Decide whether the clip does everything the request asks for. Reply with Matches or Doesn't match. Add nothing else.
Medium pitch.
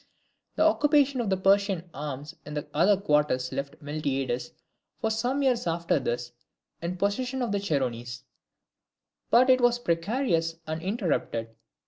Matches